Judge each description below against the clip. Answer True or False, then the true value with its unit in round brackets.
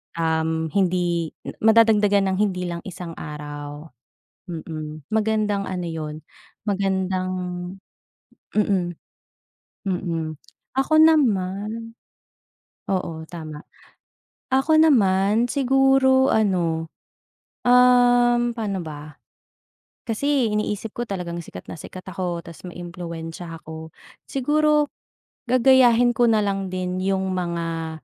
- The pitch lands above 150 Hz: True (190 Hz)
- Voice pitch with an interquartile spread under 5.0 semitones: False (5.5 semitones)